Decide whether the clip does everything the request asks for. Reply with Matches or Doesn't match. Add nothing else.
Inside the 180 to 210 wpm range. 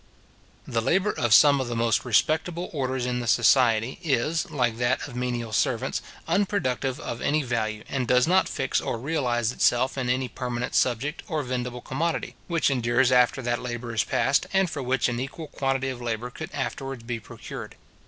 Matches